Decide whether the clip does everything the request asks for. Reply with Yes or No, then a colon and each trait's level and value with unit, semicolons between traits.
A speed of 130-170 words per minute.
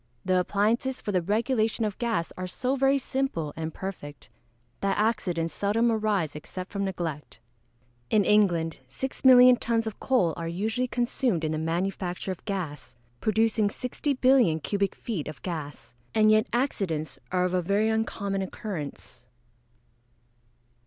Yes: average, 140 wpm